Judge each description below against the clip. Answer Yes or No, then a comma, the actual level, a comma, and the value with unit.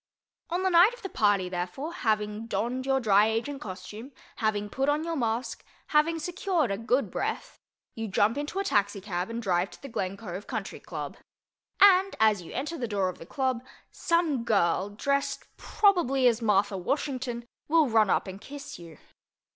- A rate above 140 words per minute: Yes, average, 175 wpm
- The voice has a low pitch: No, high, 235 Hz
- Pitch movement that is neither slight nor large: No, wide, 6.1 semitones